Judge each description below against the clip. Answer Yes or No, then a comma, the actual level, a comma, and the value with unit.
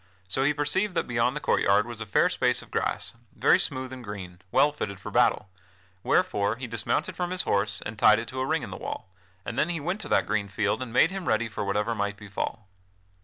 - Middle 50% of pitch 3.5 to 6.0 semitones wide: Yes, average, 5.2 semitones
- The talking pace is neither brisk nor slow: No, fast, 240 wpm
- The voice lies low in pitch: Yes, low, 115 Hz